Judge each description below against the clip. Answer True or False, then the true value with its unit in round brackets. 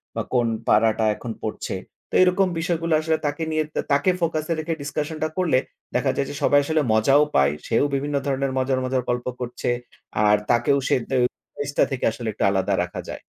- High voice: False (140 Hz)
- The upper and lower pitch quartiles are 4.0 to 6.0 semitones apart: True (4.3 semitones)